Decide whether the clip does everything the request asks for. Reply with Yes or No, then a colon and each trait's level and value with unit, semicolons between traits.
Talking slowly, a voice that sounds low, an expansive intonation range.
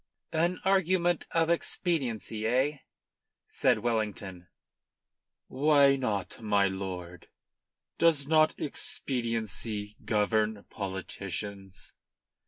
Yes: slow, 75 wpm; low, 110 Hz; wide, 6.9 semitones